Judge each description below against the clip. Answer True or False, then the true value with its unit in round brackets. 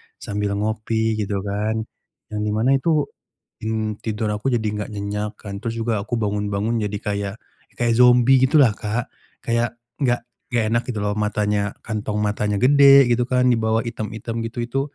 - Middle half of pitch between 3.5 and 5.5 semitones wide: False (2.4 semitones)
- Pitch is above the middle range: False (110 Hz)